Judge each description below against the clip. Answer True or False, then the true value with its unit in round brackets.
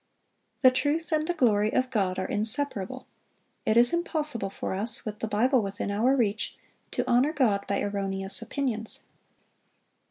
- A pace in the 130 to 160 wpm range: True (155 wpm)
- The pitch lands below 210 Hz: False (225 Hz)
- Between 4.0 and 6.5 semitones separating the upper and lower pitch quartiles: True (4.5 semitones)